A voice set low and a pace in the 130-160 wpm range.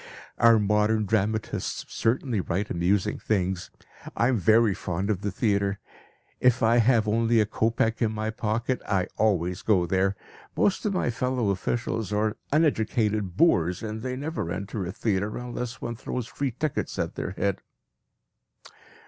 Yes: low, 110 Hz; average, 150 wpm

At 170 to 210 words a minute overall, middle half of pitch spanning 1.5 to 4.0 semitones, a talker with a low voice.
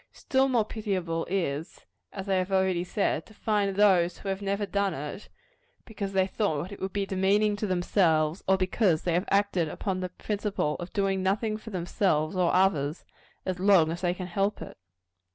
No: average, 190 wpm; narrow, 2.4 semitones; high, 190 Hz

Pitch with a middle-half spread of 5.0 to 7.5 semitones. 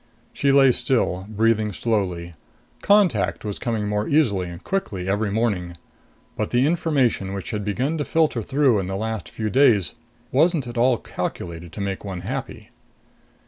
Yes: average, 5.3 semitones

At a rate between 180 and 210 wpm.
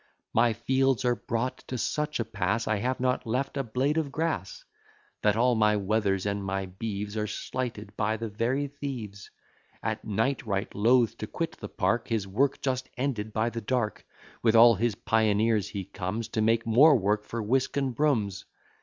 Yes: average, 185 wpm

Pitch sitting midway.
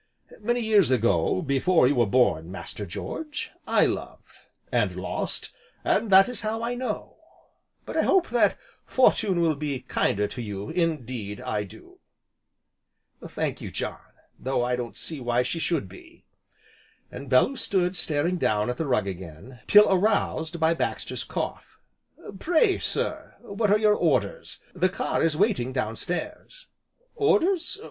Yes: medium, 160 Hz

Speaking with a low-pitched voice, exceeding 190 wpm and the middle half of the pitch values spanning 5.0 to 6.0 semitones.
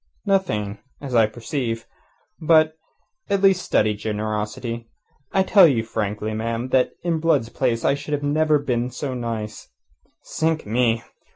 No: low, 120 Hz; average, 145 wpm; wide, 5.6 semitones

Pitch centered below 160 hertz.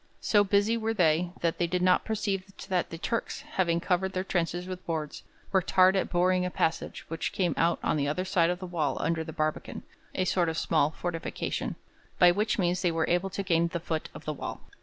No: medium, 175 Hz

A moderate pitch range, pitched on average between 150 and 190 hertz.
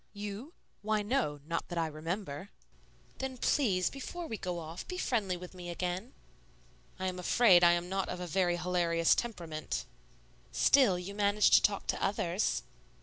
Yes: average, 3.3 semitones; medium, 185 Hz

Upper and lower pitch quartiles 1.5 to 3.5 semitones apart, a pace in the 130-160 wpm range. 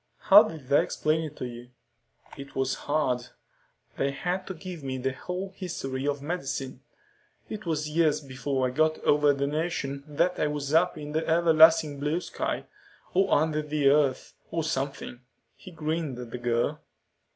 No: average, 3.1 semitones; average, 170 wpm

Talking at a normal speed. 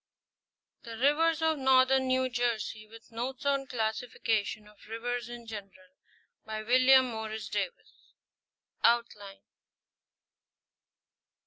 No: slow, 105 wpm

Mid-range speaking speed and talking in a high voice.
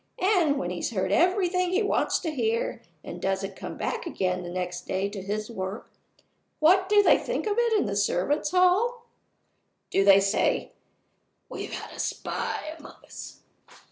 Yes: average, 170 wpm; high, 235 Hz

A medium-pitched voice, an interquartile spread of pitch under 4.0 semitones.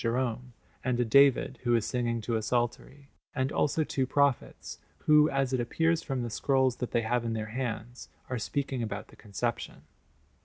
No: low, 125 Hz; narrow, 2.6 semitones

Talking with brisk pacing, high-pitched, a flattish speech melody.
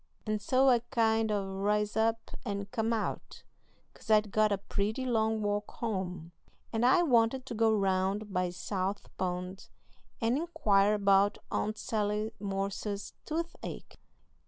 No: average, 140 wpm; high, 210 Hz; narrow, 2.3 semitones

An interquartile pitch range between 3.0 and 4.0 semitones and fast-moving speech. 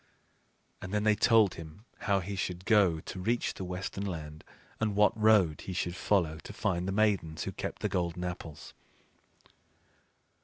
No: average, 3.4 semitones; average, 165 wpm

